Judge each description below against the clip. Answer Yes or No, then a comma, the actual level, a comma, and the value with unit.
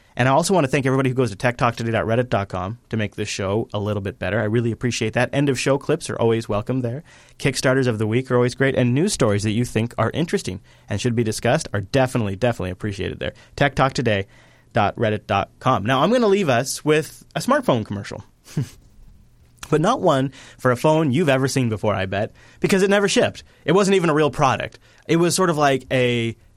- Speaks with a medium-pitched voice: No, low, 125 Hz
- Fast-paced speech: Yes, fast, 210 wpm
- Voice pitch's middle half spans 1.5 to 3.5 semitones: No, average, 4.3 semitones